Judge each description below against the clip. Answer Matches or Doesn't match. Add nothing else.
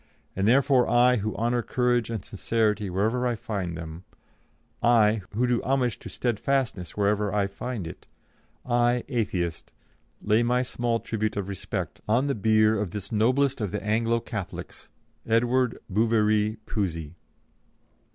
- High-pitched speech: Doesn't match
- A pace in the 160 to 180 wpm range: Doesn't match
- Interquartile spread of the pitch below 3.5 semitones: Matches